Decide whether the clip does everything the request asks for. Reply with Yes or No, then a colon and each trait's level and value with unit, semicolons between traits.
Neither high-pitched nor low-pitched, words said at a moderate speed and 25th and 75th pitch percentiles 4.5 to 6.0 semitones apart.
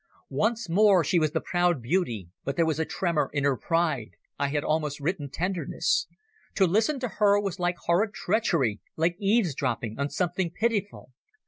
Yes: medium, 170 Hz; average, 165 wpm; average, 5.3 semitones